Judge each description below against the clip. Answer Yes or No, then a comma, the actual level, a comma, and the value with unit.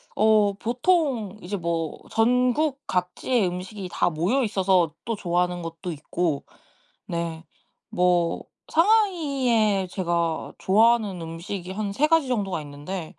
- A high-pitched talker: Yes, high, 195 Hz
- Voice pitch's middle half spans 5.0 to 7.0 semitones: Yes, wide, 5.5 semitones